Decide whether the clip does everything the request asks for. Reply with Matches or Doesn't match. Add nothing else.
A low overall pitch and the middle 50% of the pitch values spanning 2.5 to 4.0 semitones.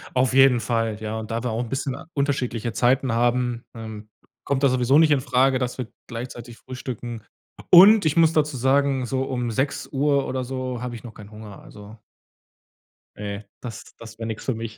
Matches